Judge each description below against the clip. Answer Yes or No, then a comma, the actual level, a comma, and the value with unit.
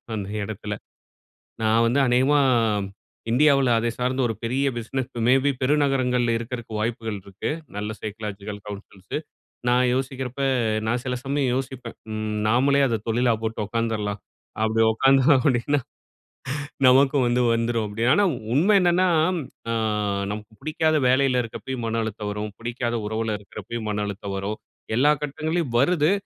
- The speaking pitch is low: Yes, low, 120 Hz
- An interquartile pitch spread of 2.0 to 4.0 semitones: Yes, average, 3.6 semitones